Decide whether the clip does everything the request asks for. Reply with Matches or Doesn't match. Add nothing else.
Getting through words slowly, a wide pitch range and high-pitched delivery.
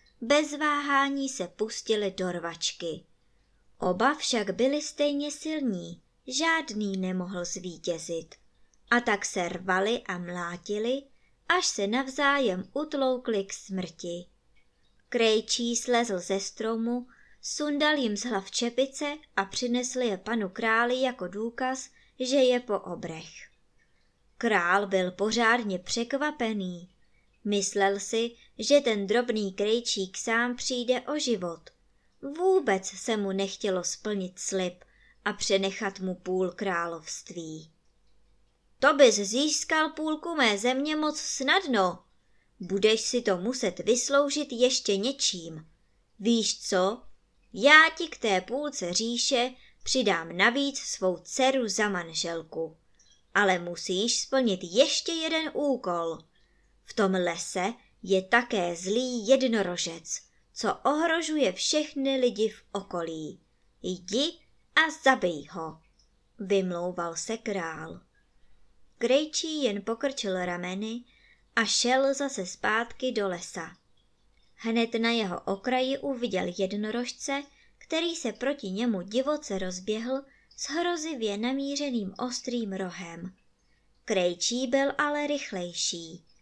Matches